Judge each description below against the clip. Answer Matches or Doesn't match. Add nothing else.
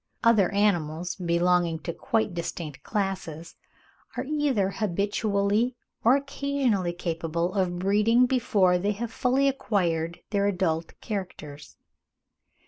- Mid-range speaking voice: Doesn't match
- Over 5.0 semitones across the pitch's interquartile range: Doesn't match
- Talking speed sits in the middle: Doesn't match